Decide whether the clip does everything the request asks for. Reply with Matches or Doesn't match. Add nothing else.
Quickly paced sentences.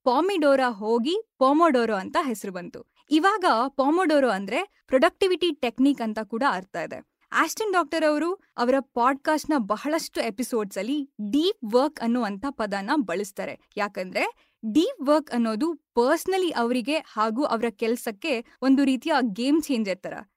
Matches